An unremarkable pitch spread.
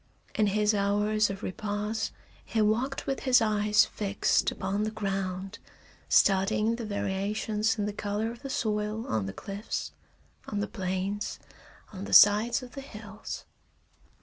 No: narrow, 1.6 semitones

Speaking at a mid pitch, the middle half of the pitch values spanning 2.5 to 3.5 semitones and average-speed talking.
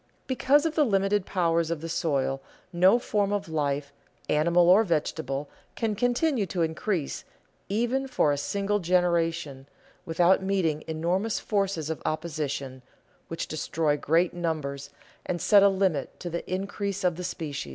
No: medium, 175 Hz; average, 4.1 semitones; average, 150 wpm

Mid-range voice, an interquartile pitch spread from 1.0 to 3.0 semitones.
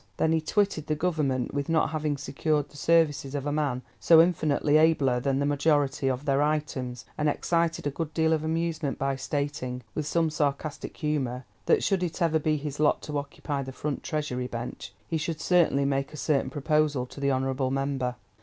Yes: medium, 145 Hz; narrow, 2.5 semitones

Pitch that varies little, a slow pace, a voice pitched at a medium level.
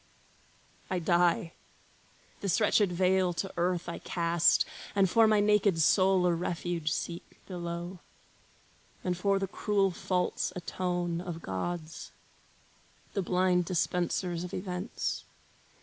Yes: narrow, 1.7 semitones; slow, 120 wpm; medium, 180 Hz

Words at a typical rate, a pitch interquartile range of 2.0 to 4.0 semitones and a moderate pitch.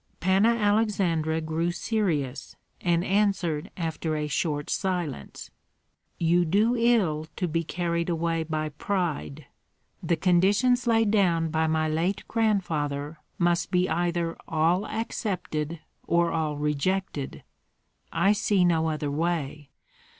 No: slow, 120 wpm; average, 3.5 semitones; medium, 170 Hz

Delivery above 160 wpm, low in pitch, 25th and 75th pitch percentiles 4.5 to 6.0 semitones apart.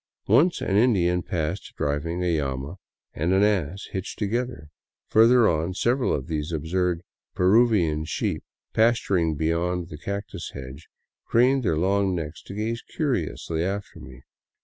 No: average, 145 wpm; very low, 90 Hz; average, 4.9 semitones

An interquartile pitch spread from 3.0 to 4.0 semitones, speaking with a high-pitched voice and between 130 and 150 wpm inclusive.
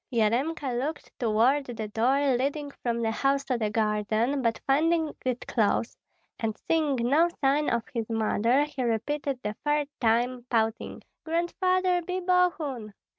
No: average, 4.6 semitones; very high, 260 Hz; average, 145 wpm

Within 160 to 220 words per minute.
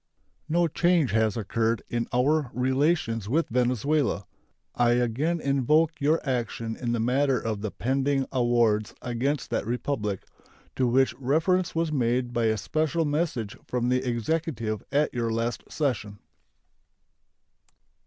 No: slow, 135 wpm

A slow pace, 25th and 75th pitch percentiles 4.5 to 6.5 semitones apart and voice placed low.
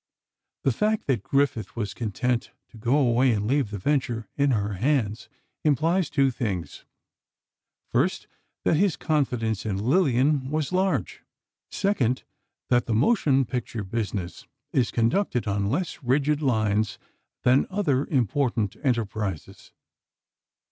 Yes: slow, 125 wpm; average, 4.8 semitones; low, 125 Hz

